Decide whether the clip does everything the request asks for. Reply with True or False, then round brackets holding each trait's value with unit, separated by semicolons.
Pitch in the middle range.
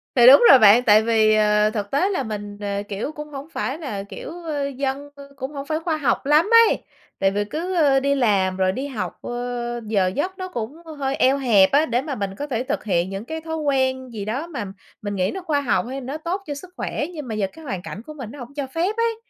False (265 Hz)